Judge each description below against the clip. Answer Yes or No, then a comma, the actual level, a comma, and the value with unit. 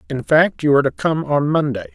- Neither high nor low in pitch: Yes, medium, 150 Hz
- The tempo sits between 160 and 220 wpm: No, fast, 245 wpm